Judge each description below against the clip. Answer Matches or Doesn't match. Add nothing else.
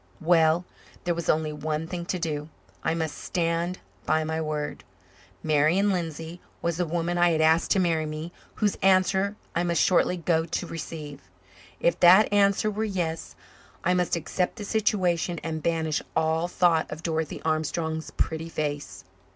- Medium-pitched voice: Matches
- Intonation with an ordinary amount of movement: Doesn't match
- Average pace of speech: Matches